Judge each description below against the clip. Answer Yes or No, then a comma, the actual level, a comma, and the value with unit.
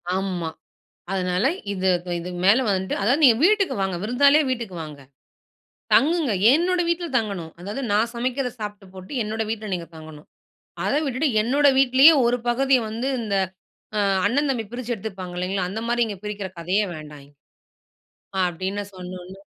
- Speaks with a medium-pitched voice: No, high, 210 Hz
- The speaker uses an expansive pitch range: Yes, wide, 5.8 semitones